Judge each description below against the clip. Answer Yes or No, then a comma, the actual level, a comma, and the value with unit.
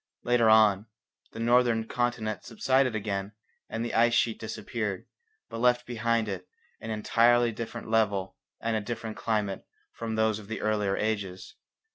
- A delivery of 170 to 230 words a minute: No, average, 150 wpm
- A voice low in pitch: Yes, low, 110 Hz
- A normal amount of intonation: No, narrow, 1.8 semitones